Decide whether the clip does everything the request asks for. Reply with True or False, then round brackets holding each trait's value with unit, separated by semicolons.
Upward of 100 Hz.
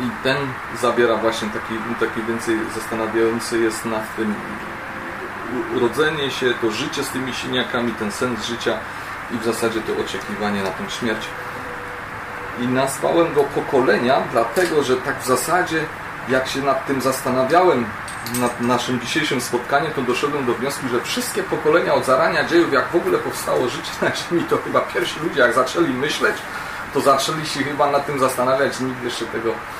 True (125 Hz)